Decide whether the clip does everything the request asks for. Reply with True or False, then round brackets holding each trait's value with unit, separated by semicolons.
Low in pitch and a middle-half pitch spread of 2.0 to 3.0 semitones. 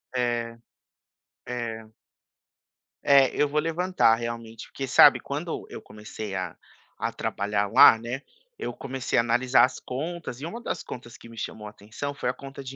False (120 Hz; 3.4 semitones)